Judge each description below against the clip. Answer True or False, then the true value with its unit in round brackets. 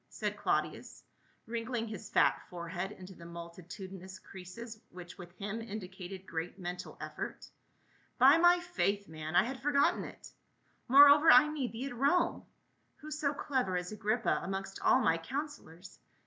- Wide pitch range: True (6.8 semitones)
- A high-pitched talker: True (205 Hz)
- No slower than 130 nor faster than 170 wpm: True (155 wpm)